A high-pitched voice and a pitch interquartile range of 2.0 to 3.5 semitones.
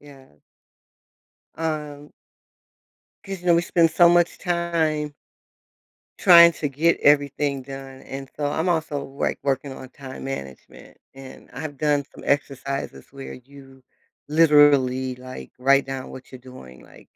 No: medium, 140 Hz; average, 2.8 semitones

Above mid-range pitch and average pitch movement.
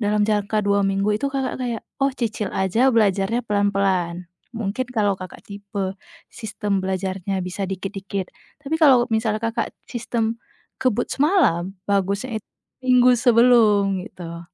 Yes: high, 205 Hz; average, 3.5 semitones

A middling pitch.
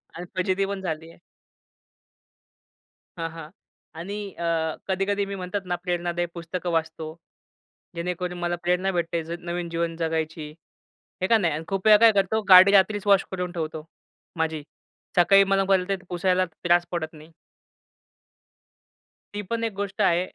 Yes: medium, 180 Hz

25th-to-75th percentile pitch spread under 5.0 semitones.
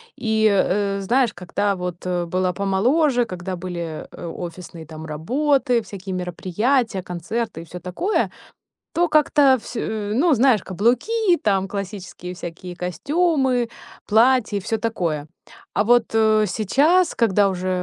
No: wide, 5.5 semitones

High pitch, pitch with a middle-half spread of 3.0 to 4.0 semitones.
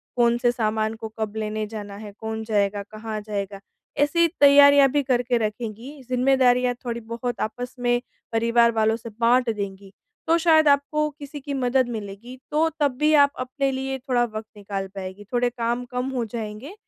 Yes: high, 240 Hz; average, 3.6 semitones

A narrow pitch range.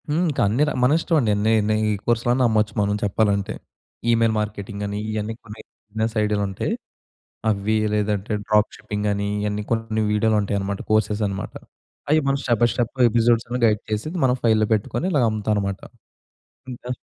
Yes: narrow, 2.2 semitones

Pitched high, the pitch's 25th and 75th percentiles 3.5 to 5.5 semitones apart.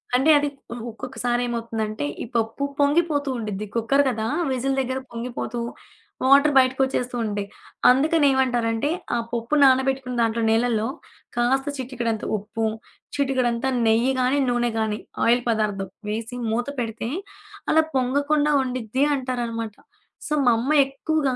No: high, 245 Hz; average, 2.8 semitones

